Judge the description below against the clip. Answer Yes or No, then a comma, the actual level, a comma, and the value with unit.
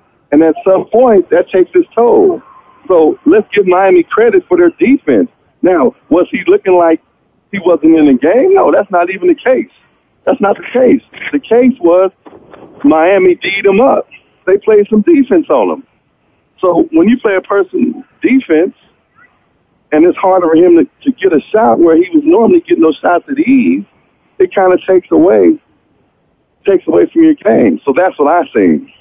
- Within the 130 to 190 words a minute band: Yes, average, 185 wpm